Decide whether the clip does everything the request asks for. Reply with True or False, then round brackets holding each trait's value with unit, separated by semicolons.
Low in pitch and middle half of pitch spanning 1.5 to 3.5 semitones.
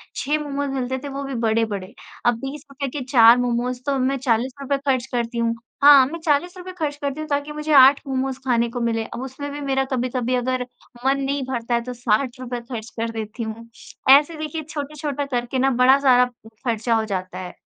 False (260 Hz; 3.1 semitones)